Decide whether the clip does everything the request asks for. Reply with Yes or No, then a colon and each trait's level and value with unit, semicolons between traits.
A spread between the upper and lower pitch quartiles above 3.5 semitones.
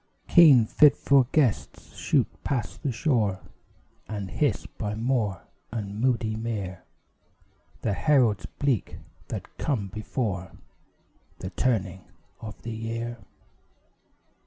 Yes: average, 4.1 semitones